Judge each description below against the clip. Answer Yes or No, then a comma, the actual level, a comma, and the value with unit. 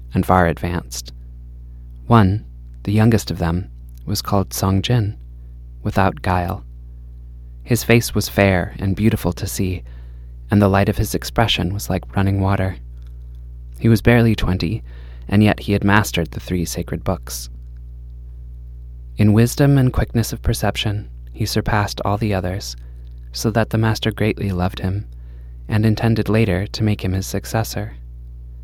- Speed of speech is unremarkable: Yes, average, 150 wpm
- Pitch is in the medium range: No, very low, 90 Hz